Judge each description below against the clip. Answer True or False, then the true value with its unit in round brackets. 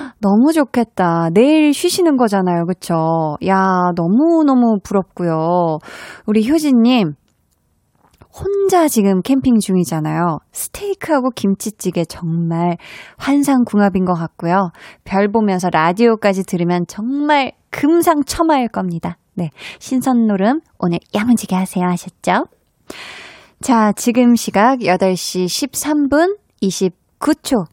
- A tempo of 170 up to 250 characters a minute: True (240 characters per minute)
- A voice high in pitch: True (200 Hz)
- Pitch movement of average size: False (6.8 semitones)